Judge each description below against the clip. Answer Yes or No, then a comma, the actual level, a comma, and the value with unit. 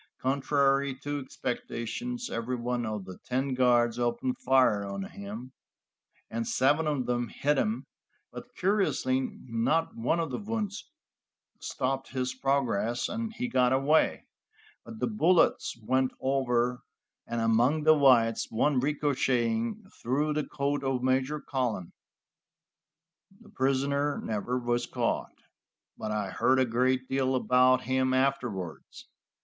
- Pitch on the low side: Yes, low, 130 Hz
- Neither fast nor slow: No, slow, 130 wpm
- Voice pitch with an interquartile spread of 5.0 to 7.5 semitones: No, average, 2.9 semitones